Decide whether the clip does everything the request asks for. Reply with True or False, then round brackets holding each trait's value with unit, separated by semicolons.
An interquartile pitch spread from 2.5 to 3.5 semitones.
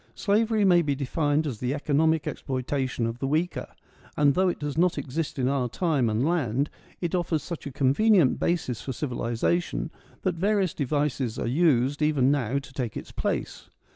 False (4.5 semitones)